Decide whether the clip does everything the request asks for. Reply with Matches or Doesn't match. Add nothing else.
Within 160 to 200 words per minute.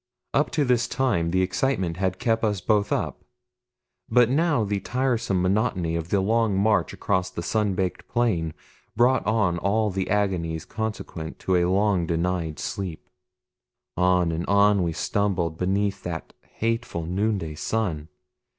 Doesn't match